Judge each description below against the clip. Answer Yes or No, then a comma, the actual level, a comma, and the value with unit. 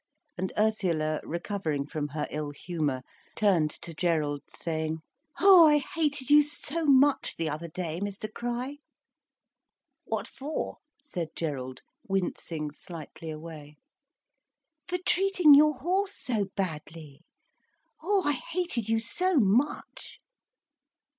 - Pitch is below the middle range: No, high, 195 Hz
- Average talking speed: No, slow, 115 wpm